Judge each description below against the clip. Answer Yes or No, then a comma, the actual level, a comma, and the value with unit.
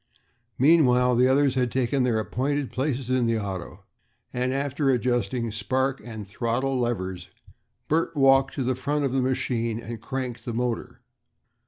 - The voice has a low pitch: Yes, low, 125 Hz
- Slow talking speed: No, average, 155 wpm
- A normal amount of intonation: No, narrow, 2.3 semitones